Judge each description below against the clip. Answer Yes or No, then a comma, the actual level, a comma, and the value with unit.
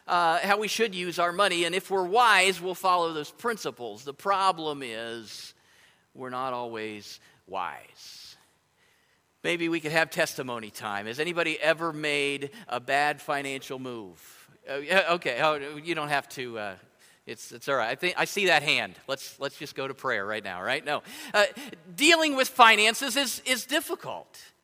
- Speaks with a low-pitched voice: No, medium, 165 Hz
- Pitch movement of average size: No, wide, 6.2 semitones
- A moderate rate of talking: Yes, average, 175 wpm